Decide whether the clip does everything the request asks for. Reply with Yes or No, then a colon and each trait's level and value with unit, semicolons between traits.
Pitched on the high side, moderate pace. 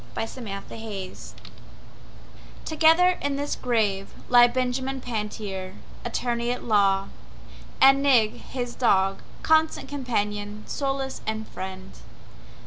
No: high, 235 Hz; slow, 100 wpm